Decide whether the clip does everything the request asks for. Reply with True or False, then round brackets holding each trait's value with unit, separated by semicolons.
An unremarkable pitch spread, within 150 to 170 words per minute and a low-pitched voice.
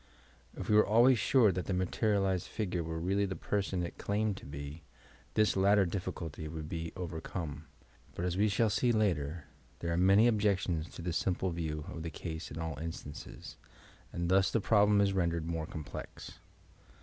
False (3.8 semitones; 185 wpm; 90 Hz)